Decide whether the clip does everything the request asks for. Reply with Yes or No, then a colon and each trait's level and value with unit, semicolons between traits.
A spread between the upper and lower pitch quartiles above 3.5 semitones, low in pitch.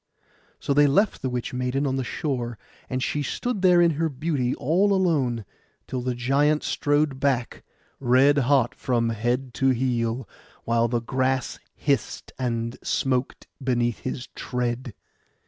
No: average, 3.0 semitones; low, 130 Hz